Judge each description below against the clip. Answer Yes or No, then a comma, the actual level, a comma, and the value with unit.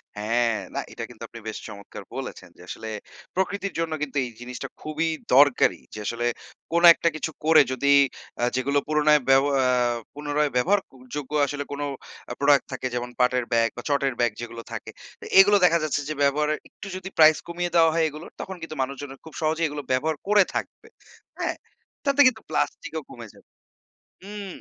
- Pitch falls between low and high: Yes, medium, 145 Hz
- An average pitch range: Yes, average, 4.3 semitones